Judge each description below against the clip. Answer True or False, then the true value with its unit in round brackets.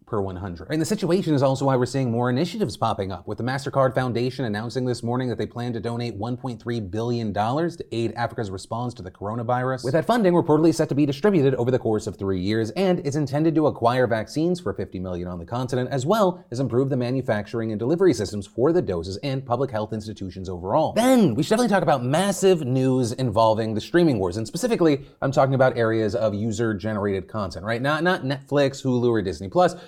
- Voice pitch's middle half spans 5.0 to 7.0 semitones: True (5.3 semitones)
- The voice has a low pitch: True (125 Hz)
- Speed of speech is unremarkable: False (215 wpm)